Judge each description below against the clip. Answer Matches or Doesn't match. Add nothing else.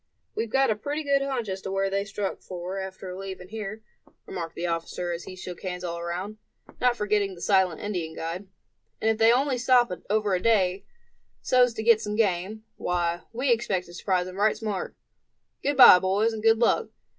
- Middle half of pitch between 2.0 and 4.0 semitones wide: Matches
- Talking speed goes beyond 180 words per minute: Matches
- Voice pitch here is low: Doesn't match